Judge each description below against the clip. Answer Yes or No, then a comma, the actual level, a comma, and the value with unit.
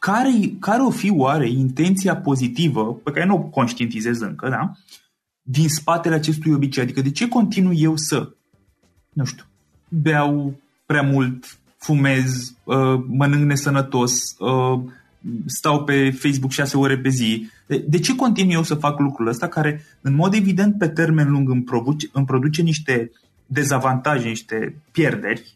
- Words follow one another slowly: No, average, 145 wpm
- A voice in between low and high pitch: Yes, medium, 145 Hz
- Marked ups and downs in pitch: No, average, 3.9 semitones